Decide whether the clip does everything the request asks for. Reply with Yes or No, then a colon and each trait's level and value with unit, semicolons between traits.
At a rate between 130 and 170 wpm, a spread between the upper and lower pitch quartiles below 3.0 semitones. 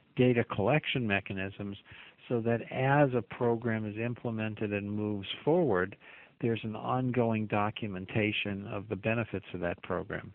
Yes: slow, 135 wpm; narrow, 2.6 semitones